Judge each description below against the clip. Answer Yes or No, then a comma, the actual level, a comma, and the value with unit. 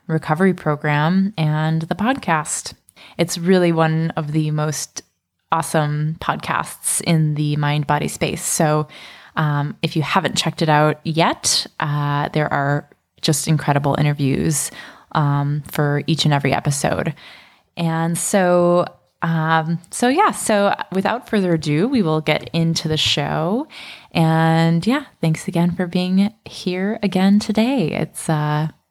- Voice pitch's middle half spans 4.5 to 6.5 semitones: No, average, 3.2 semitones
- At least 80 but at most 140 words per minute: Yes, slow, 135 wpm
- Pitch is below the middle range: No, medium, 160 Hz